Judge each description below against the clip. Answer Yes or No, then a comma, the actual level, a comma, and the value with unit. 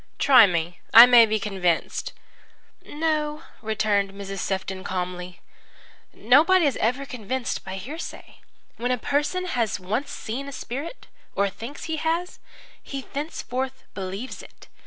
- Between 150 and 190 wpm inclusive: No, slow, 135 wpm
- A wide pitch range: Yes, wide, 6.5 semitones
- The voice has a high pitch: Yes, high, 240 Hz